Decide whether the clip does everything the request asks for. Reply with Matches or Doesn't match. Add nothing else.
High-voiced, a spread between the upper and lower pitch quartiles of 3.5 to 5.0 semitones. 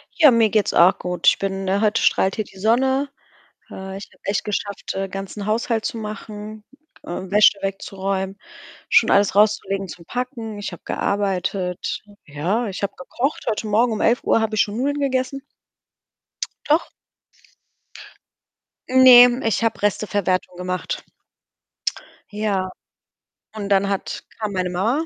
Doesn't match